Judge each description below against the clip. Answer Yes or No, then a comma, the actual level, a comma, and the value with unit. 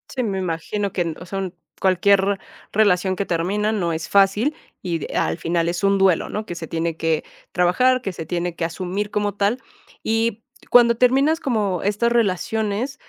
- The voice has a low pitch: No, high, 195 Hz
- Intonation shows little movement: No, average, 3.8 semitones